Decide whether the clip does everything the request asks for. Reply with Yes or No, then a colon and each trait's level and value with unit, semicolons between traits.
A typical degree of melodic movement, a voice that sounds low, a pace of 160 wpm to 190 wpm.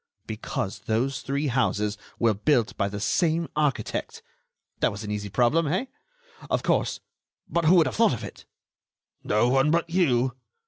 No: wide, 6.4 semitones; low, 130 Hz; average, 165 wpm